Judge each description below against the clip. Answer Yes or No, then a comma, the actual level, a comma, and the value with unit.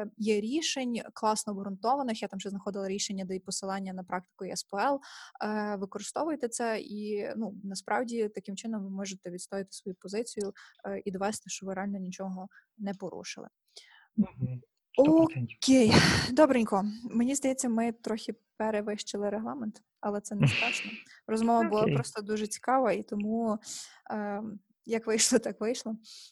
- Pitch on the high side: Yes, high, 210 Hz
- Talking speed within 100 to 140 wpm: Yes, average, 130 wpm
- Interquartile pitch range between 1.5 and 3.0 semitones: Yes, narrow, 2.6 semitones